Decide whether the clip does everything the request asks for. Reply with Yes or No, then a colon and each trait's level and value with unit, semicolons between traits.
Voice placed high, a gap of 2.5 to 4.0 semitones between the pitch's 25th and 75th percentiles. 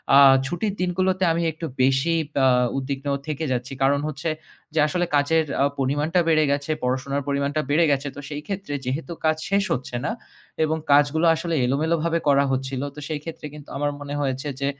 No: medium, 145 Hz; average, 2.9 semitones